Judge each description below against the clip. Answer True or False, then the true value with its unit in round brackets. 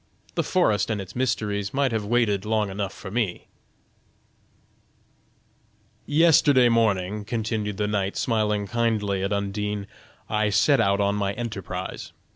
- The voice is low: True (105 Hz)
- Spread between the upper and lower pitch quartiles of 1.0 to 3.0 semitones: True (2.5 semitones)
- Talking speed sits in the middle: False (130 wpm)